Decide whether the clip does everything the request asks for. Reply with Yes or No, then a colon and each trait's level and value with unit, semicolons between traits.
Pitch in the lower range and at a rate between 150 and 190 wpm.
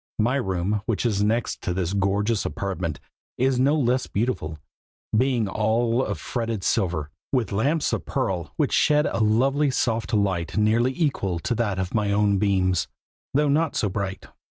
Yes: low, 110 Hz; average, 165 wpm